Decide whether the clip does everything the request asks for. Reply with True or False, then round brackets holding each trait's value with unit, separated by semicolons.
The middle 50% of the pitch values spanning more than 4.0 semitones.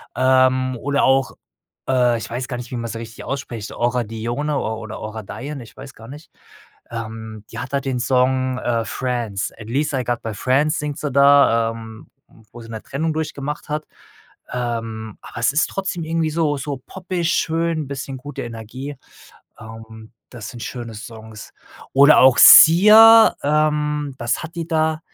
True (4.5 semitones)